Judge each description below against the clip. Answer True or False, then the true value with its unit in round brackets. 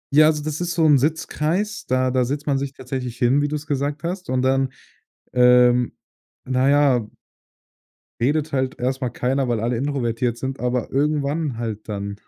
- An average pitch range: True (3.0 semitones)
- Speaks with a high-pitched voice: False (135 Hz)